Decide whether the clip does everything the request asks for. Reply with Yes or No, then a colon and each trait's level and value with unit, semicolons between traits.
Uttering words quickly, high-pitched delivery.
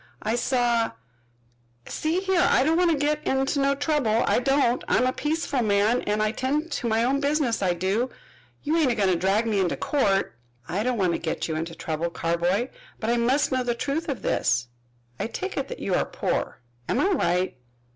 Yes: fast, 210 wpm; high, 240 Hz